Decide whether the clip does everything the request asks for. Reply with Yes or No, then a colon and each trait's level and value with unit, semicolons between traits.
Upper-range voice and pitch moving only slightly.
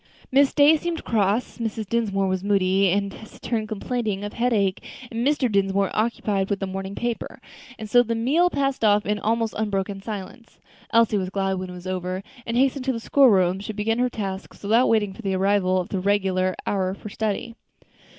No: high, 205 Hz; average, 3.2 semitones